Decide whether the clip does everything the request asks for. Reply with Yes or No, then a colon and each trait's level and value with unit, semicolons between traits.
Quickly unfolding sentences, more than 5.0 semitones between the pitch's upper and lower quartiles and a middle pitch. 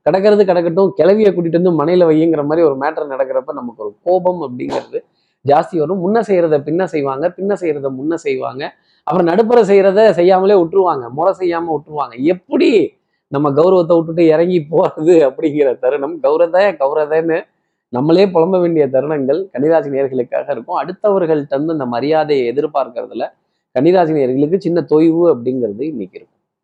No: fast, 135 wpm; average, 4.2 semitones; medium, 170 Hz